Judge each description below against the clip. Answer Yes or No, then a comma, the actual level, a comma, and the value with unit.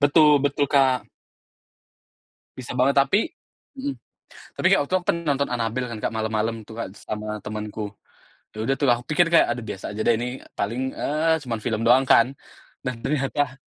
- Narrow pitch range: No, average, 4.5 semitones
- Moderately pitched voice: No, low, 125 Hz